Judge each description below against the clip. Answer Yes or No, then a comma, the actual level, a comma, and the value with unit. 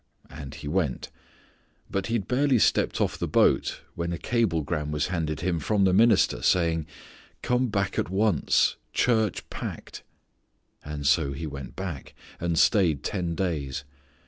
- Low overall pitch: Yes, very low, 85 Hz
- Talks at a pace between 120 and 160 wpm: Yes, average, 145 wpm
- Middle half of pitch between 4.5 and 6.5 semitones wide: Yes, average, 5.0 semitones